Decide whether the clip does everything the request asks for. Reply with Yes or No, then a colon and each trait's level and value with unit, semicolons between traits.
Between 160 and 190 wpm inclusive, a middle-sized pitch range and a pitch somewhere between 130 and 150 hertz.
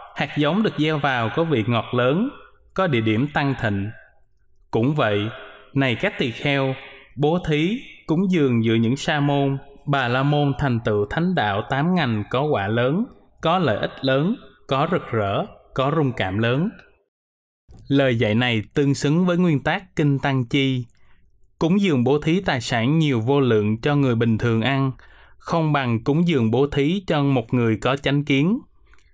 Yes: average, 180 wpm; average, 4.8 semitones; medium, 140 Hz